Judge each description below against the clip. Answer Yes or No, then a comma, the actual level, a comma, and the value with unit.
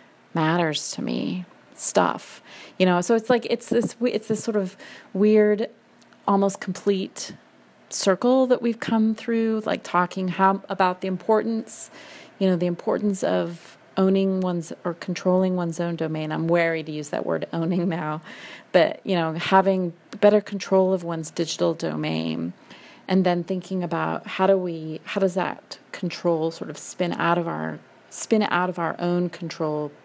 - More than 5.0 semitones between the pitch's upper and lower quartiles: No, average, 3.7 semitones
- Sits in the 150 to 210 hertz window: Yes, medium, 185 Hz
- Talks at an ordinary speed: Yes, average, 165 wpm